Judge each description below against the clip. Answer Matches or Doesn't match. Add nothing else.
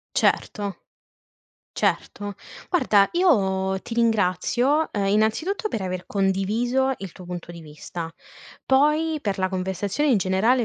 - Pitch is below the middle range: Doesn't match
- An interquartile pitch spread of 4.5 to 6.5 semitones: Matches